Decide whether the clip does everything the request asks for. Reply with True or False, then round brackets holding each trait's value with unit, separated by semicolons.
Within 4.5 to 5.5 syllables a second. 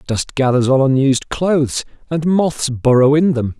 True (4.7 syllables/s)